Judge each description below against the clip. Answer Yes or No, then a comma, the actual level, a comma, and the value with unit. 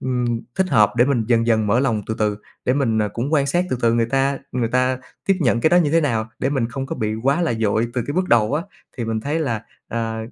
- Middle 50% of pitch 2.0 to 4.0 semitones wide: Yes, average, 3.7 semitones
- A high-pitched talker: No, low, 120 Hz